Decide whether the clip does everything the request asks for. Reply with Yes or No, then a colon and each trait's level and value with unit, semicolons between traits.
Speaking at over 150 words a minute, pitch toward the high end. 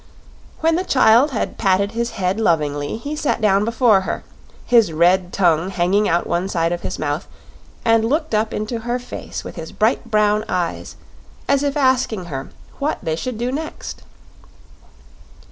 Yes: average, 165 wpm; high, 215 Hz